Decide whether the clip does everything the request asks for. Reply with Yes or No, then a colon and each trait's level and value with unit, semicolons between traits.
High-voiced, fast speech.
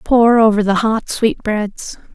No: high, 215 Hz; average, 140 wpm